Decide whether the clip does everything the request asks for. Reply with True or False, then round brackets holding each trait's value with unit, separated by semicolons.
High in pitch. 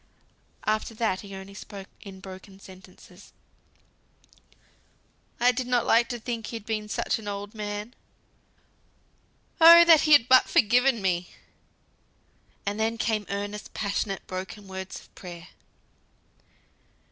True (210 Hz)